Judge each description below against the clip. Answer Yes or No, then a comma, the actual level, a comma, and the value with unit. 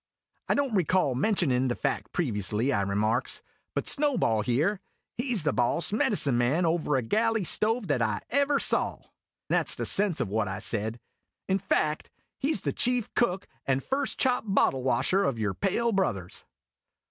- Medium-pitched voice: Yes, medium, 155 Hz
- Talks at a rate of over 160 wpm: Yes, average, 180 wpm